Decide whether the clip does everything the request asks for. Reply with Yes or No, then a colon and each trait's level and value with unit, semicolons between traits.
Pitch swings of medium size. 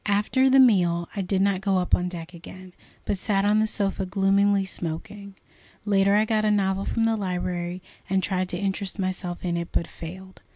No: narrow, 2.0 semitones